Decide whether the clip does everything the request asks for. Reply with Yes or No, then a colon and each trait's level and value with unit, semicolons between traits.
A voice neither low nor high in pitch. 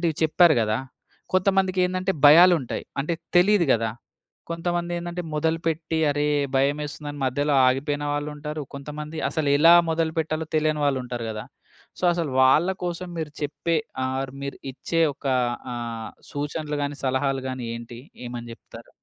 Yes: medium, 150 Hz